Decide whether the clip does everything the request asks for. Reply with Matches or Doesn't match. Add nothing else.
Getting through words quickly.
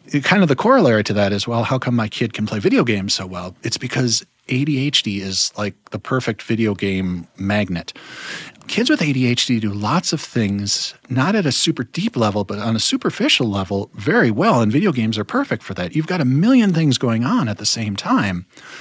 Matches